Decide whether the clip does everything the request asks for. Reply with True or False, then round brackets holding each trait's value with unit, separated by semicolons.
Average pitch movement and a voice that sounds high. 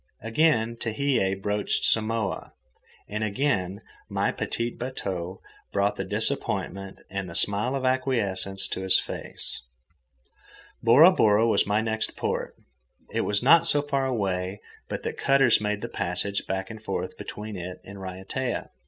False (4.0 semitones; 105 Hz)